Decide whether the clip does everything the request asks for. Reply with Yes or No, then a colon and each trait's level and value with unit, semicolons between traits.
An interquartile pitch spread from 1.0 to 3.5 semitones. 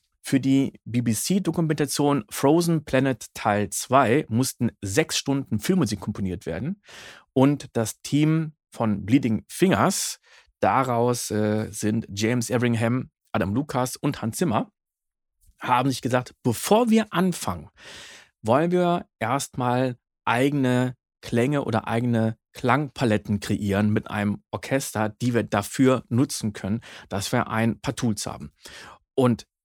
No: average, 4.2 semitones